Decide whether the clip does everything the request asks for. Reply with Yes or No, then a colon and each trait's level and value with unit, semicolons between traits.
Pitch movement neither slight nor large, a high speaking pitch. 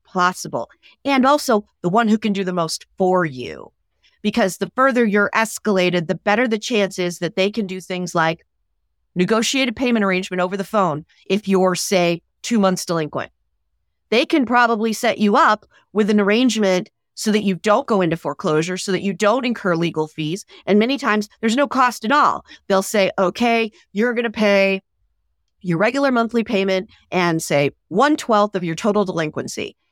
Yes: average, 3.9 semitones; high, 195 Hz